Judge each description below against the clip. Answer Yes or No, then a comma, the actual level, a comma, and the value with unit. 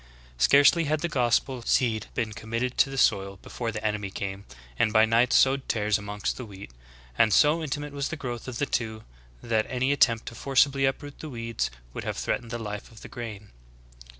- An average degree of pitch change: Yes, average, 3.9 semitones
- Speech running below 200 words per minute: No, fast, 205 wpm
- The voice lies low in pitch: Yes, low, 115 Hz